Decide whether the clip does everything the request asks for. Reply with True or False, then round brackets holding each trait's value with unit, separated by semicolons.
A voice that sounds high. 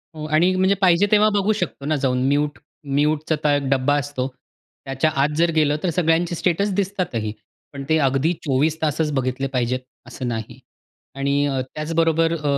False (150 Hz)